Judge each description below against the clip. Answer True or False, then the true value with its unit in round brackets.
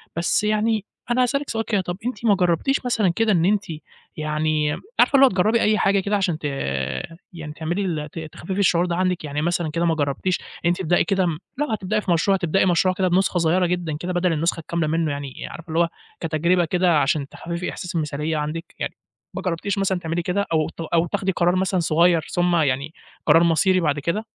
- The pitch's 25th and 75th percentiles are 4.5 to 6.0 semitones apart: False (3.2 semitones)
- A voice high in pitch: False (175 Hz)